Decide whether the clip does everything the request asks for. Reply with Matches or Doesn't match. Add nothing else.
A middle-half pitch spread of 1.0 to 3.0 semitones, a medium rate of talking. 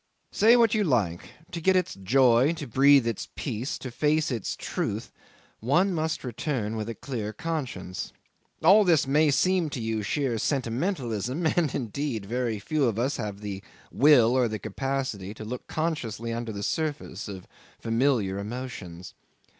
Doesn't match